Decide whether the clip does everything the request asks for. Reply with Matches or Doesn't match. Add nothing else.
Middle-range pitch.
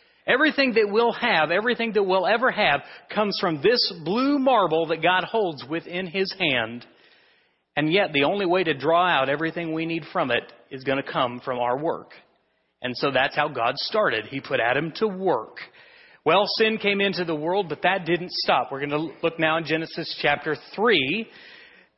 Matches